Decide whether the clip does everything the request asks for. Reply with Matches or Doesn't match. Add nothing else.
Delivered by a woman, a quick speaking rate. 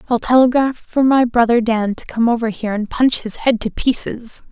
Matches